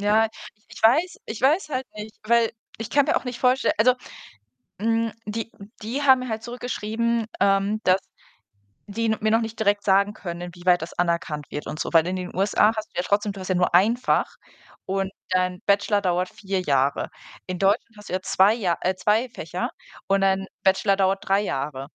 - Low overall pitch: No, high, 205 Hz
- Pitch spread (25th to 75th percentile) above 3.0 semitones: Yes, average, 3.6 semitones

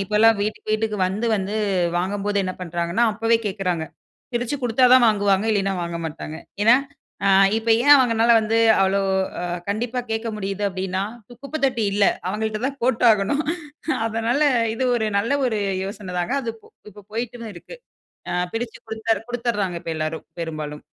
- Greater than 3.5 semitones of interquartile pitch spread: No, average, 3.2 semitones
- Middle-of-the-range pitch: No, high, 215 Hz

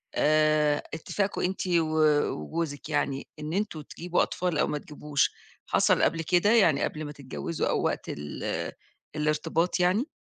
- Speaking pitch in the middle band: Yes, medium, 155 Hz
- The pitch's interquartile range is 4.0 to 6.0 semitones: No, average, 3.1 semitones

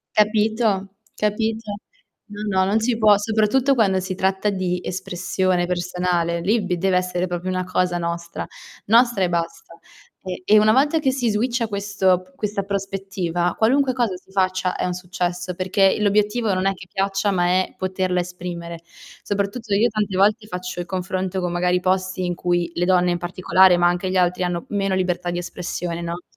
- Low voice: No, medium, 185 Hz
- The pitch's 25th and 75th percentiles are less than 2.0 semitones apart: No, narrow, 2.5 semitones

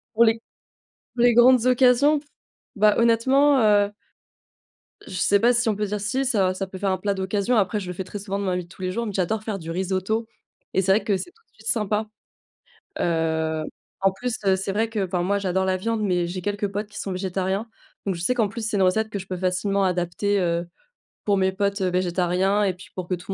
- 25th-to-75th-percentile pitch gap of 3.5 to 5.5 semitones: No, average, 2.9 semitones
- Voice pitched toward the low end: No, high, 200 Hz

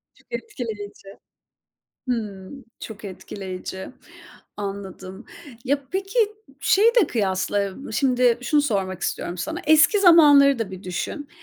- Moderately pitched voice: No, high, 225 Hz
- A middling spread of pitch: No, wide, 7.1 semitones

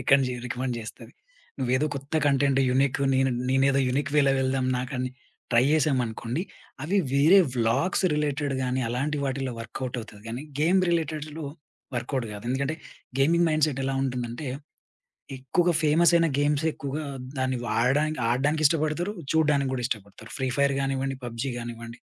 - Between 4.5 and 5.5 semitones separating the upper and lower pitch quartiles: No, average, 3.1 semitones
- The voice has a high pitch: No, low, 135 Hz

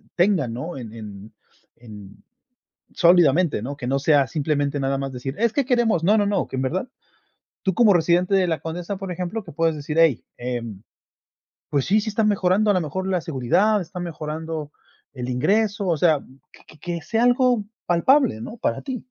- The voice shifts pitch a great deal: Yes, wide, 6.5 semitones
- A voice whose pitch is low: No, medium, 165 Hz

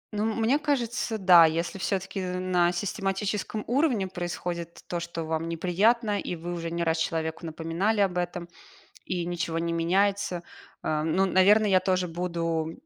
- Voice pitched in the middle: Yes, medium, 180 Hz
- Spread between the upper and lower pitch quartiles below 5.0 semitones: Yes, average, 3.1 semitones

